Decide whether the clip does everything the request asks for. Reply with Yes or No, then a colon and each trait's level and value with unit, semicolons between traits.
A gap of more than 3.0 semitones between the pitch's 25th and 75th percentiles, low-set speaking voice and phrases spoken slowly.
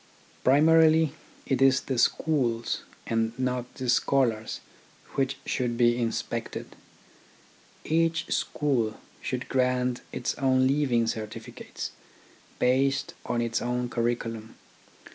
No: narrow, 2.6 semitones; low, 125 Hz; slow, 105 wpm